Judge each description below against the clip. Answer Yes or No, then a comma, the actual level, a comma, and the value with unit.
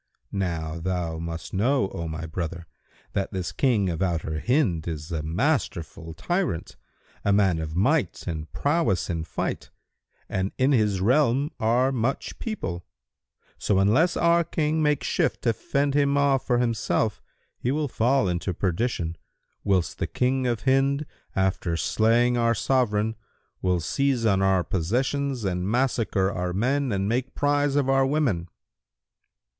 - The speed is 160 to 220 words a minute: No, average, 150 wpm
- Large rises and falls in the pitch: Yes, wide, 7.3 semitones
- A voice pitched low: Yes, low, 110 Hz